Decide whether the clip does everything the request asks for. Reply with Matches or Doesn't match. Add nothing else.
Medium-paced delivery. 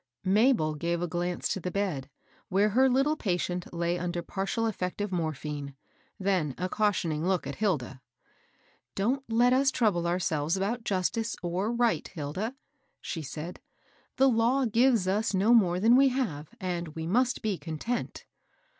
Matches